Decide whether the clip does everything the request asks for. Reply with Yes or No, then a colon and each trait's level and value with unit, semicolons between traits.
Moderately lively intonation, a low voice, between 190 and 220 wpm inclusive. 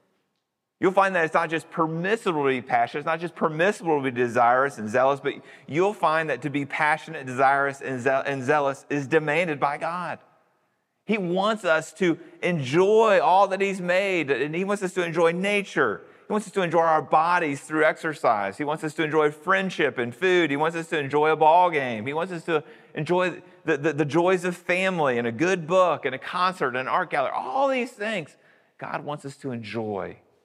No: average, 3.8 semitones; medium, 160 Hz; fast, 205 wpm